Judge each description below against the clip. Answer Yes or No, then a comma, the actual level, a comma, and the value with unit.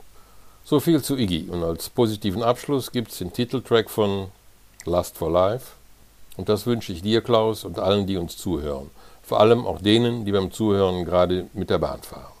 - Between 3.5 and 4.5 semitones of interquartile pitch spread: Yes, average, 3.8 semitones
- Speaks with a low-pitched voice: Yes, low, 105 Hz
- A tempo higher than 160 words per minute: Yes, fast, 190 wpm